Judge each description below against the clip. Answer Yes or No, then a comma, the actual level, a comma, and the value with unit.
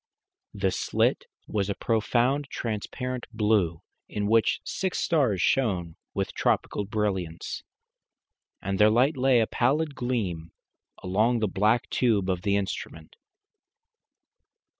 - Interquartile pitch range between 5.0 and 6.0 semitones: No, average, 4.3 semitones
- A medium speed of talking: No, slow, 120 wpm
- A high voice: No, low, 110 Hz